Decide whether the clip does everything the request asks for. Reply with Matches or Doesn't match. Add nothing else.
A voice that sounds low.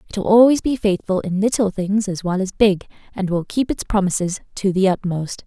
Doesn't match